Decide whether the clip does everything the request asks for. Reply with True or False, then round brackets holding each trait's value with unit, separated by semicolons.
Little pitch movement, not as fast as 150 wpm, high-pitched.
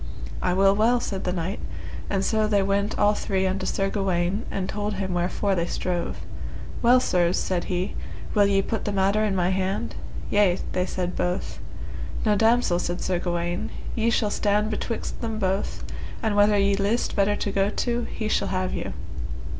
False (2.2 semitones; 185 wpm; 195 Hz)